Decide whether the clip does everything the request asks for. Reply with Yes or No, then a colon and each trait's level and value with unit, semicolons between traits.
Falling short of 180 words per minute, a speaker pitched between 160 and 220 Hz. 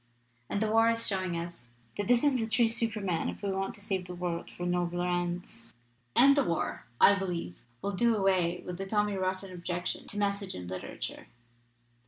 No: average, 195 wpm; high, 190 Hz